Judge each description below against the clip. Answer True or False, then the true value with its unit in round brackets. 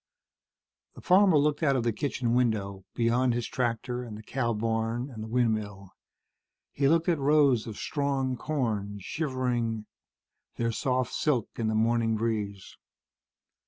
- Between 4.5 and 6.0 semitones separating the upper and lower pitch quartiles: False (3.3 semitones)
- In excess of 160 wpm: False (145 wpm)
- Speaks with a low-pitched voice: True (120 Hz)